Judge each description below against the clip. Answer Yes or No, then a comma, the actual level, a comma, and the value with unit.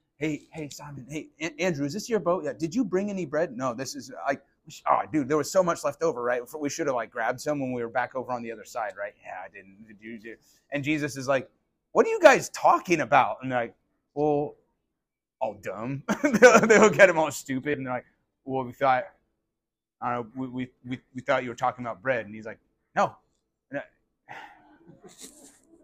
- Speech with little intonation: No, average, 4.7 semitones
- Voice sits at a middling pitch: Yes, medium, 145 Hz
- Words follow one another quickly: Yes, fast, 215 wpm